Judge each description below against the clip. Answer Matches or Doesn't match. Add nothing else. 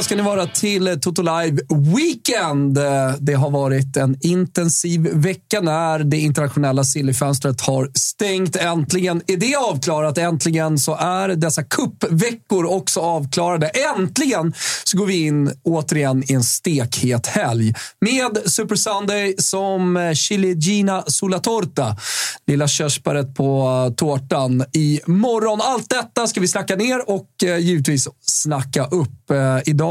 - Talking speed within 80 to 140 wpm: Matches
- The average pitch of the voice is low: Doesn't match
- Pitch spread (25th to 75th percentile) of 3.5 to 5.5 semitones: Matches